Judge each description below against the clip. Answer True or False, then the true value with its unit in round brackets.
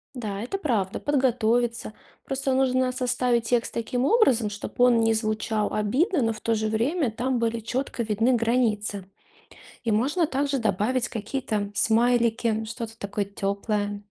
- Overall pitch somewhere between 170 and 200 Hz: False (230 Hz)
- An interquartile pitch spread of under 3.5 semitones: True (2.9 semitones)